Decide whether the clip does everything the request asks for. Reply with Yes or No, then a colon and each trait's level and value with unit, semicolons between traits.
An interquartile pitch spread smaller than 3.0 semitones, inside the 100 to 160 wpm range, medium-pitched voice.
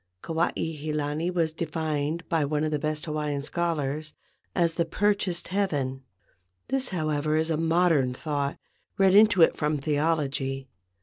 Yes: narrow, 2.4 semitones; average, 150 wpm; medium, 155 Hz